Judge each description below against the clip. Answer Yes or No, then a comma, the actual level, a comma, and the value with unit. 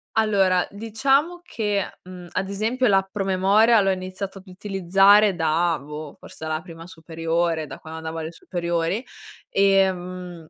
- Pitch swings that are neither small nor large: Yes, average, 3.3 semitones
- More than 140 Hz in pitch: Yes, medium, 185 Hz